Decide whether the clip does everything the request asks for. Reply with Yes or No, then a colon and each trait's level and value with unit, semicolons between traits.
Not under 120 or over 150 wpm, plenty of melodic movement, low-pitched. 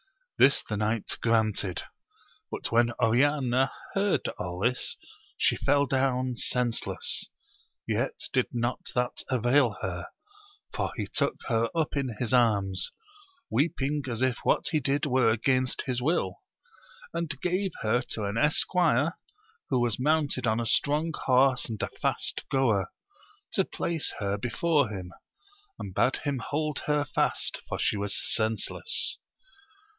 No: average, 140 wpm; average, 4.4 semitones; low, 125 Hz